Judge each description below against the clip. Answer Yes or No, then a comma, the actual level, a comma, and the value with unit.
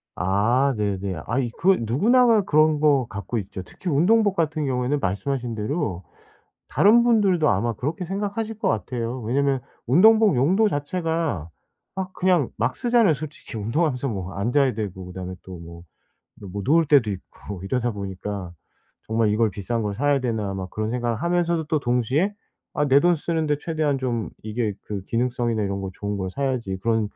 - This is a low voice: Yes, low, 125 Hz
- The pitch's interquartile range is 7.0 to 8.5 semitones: Yes, wide, 7.4 semitones